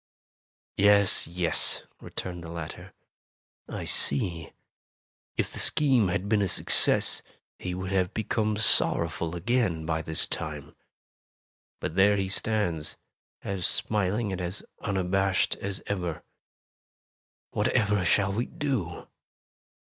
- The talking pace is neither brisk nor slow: No, slow, 115 wpm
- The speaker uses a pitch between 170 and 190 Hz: No, very low, 95 Hz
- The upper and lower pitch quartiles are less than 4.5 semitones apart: Yes, average, 3.1 semitones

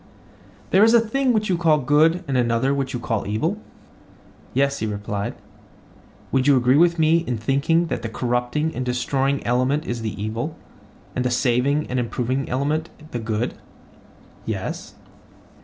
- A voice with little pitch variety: No, average, 4.5 semitones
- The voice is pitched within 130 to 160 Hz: Yes, low, 135 Hz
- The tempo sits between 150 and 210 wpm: Yes, average, 160 wpm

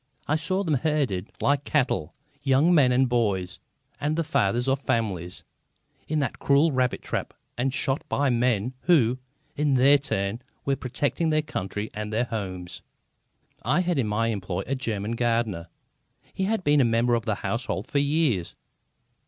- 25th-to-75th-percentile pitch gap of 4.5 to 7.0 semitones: Yes, average, 4.9 semitones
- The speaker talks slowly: No, average, 165 wpm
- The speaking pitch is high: No, low, 125 Hz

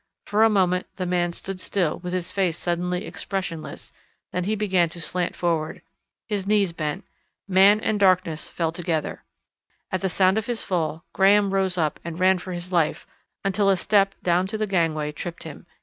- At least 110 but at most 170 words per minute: No, average, 185 wpm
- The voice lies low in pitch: No, medium, 185 Hz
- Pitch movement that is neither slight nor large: No, narrow, 2.3 semitones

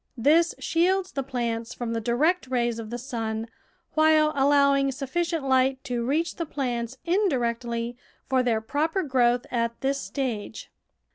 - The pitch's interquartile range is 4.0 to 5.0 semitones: Yes, average, 4.4 semitones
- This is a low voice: No, very high, 260 Hz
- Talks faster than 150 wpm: No, average, 145 wpm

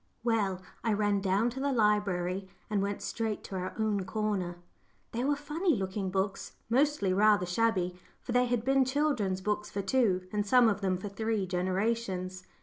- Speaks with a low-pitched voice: No, high, 205 Hz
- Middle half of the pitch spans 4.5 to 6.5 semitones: No, average, 3.6 semitones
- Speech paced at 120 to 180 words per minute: Yes, average, 175 wpm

